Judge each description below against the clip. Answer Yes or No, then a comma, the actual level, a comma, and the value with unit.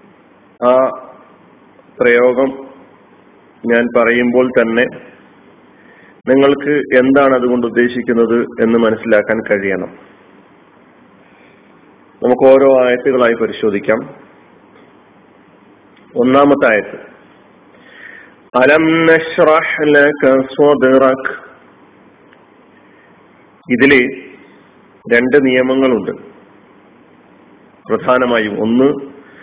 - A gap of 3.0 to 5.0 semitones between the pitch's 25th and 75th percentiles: No, narrow, 2.6 semitones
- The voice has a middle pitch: No, low, 125 Hz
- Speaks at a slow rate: Yes, slow, 50 wpm